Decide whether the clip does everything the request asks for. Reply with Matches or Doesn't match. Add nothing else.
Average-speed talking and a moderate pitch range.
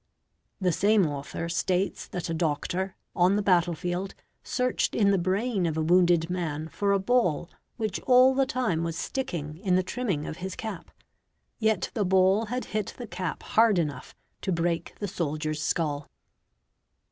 Matches